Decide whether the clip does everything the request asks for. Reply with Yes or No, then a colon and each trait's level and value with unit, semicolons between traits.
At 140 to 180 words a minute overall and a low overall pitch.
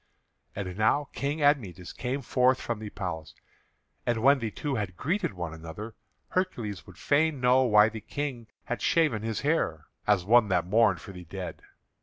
Yes: average, 175 wpm; low, 110 Hz